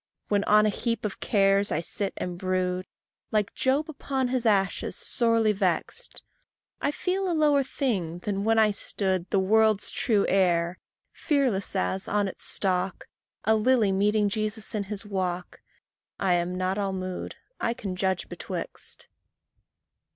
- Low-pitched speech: No, high, 200 Hz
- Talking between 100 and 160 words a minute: Yes, average, 150 wpm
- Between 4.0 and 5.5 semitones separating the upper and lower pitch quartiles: No, average, 3.1 semitones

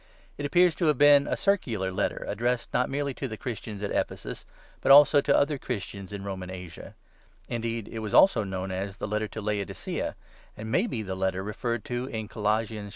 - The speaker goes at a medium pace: No, fast, 210 wpm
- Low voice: Yes, low, 110 Hz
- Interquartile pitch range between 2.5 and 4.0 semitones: No, average, 5.2 semitones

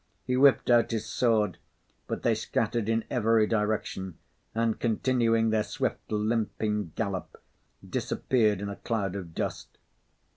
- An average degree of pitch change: No, narrow, 1.8 semitones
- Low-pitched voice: Yes, low, 110 Hz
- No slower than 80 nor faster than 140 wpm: Yes, slow, 135 wpm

